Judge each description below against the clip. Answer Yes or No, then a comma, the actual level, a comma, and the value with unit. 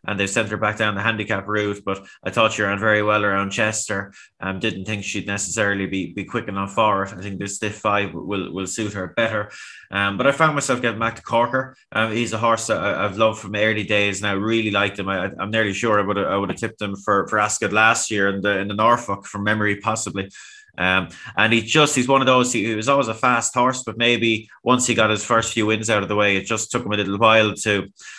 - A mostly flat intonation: Yes, narrow, 2.3 semitones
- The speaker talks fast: Yes, fast, 260 wpm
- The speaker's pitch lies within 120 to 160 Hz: No, low, 105 Hz